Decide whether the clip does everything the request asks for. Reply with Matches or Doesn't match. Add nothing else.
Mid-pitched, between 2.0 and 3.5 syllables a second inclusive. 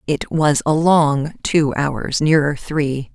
Matches